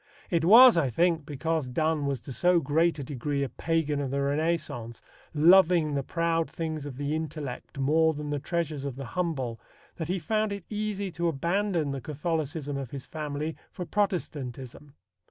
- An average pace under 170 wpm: No, average, 175 wpm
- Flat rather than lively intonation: No, average, 3.3 semitones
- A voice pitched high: No, medium, 155 Hz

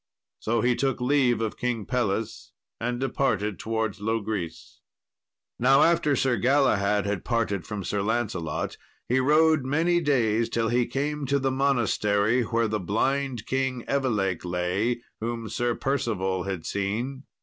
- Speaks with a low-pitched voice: Yes, low, 115 Hz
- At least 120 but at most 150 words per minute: Yes, average, 140 wpm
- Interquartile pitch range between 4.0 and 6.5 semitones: Yes, average, 4.4 semitones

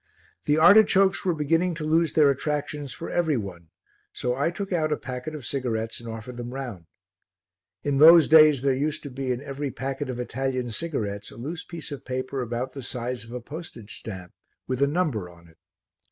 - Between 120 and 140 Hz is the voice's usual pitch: Yes, low, 135 Hz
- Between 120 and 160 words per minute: No, average, 195 wpm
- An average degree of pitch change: Yes, average, 4.2 semitones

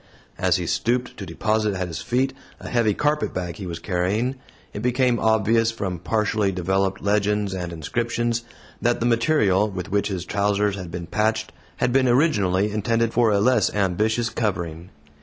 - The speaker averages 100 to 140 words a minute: No, average, 165 wpm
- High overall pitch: No, low, 105 Hz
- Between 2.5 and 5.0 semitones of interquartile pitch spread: Yes, average, 3.8 semitones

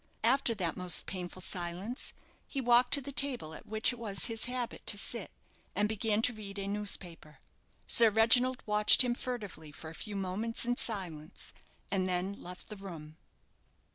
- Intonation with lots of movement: No, average, 4.4 semitones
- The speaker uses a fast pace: No, average, 170 wpm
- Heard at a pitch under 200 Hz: No, high, 210 Hz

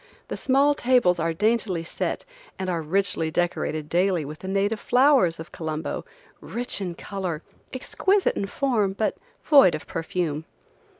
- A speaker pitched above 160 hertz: Yes, high, 190 Hz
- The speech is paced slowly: No, average, 145 wpm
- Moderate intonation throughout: No, wide, 6.2 semitones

